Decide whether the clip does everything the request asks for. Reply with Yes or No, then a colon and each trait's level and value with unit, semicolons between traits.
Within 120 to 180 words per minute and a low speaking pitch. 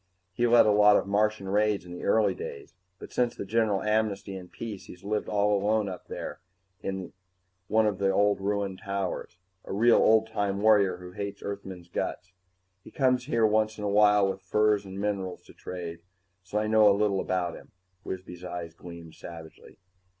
No: average, 190 wpm; low, 100 Hz